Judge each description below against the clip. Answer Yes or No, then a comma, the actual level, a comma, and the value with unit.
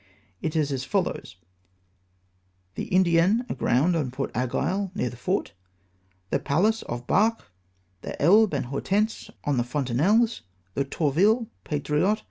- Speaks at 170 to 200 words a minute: No, average, 140 wpm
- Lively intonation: Yes, wide, 8.2 semitones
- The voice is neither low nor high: Yes, medium, 150 Hz